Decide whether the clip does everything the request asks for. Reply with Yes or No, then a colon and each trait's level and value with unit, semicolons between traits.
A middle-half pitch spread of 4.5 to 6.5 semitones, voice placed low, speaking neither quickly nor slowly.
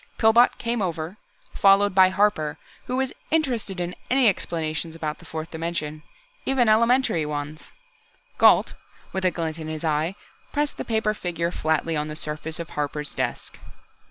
No: wide, 5.5 semitones; medium, 170 Hz; average, 155 wpm